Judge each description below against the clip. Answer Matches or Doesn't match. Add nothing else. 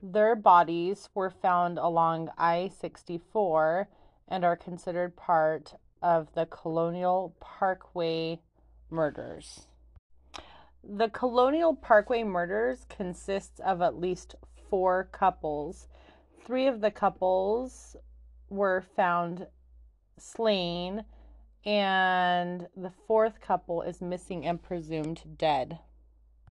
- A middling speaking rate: Doesn't match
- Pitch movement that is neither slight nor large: Matches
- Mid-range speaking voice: Matches